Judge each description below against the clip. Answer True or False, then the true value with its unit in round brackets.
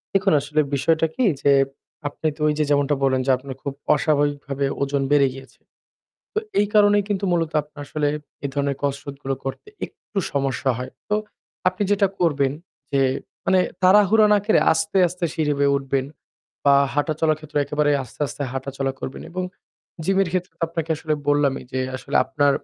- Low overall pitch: False (145 Hz)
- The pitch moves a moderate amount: True (3.5 semitones)